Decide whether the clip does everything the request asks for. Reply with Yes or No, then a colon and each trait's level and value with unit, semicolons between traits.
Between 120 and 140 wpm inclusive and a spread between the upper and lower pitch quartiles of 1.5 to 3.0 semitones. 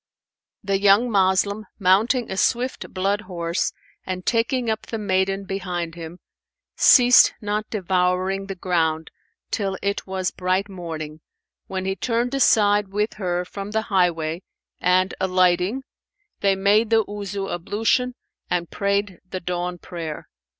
Yes: slow, 135 wpm; narrow, 2.4 semitones